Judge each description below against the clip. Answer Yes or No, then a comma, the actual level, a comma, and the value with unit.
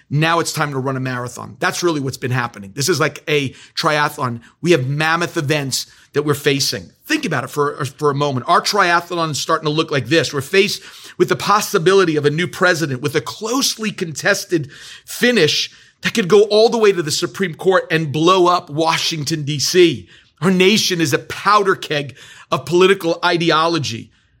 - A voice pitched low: No, medium, 160 Hz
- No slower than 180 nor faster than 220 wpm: Yes, average, 190 wpm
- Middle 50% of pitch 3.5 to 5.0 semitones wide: Yes, average, 4.2 semitones